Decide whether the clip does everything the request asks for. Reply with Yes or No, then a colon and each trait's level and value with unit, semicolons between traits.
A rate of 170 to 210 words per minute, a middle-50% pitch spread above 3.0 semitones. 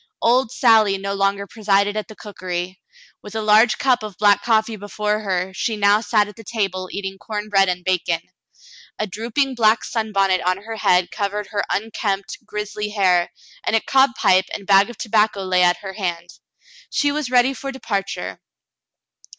No: average, 175 wpm; narrow, 2.4 semitones